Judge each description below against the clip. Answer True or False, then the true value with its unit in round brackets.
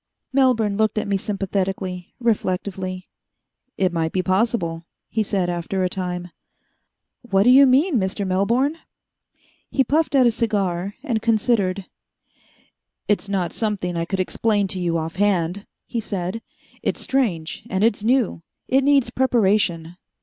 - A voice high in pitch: True (200 Hz)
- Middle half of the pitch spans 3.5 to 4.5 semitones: True (4.0 semitones)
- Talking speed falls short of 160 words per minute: True (140 wpm)